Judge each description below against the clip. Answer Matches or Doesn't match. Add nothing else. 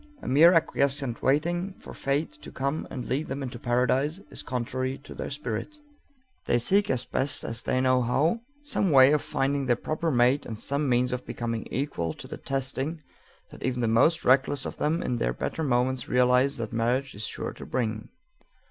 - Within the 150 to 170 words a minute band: Doesn't match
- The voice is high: Doesn't match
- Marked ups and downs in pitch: Doesn't match